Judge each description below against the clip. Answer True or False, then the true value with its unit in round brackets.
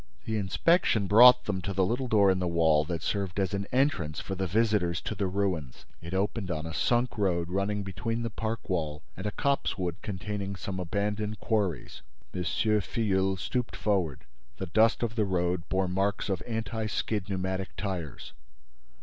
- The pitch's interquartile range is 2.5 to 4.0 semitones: True (3.1 semitones)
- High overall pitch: False (95 Hz)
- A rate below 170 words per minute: False (175 wpm)